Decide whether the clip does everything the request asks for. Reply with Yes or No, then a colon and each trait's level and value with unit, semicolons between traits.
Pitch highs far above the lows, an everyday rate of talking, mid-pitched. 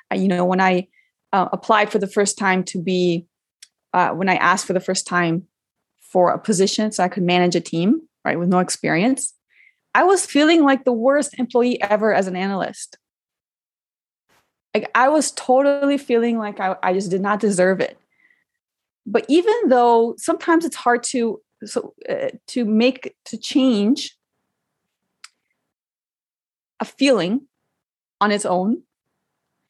No: wide, 6.4 semitones; average, 150 wpm; high, 225 Hz